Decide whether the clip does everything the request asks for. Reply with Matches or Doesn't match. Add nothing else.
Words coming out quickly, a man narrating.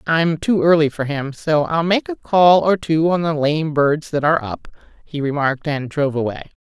Doesn't match